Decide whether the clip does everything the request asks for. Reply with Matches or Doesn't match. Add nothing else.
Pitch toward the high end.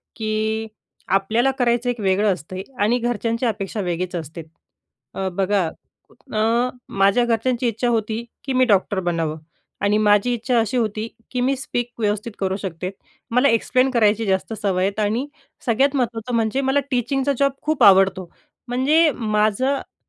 Matches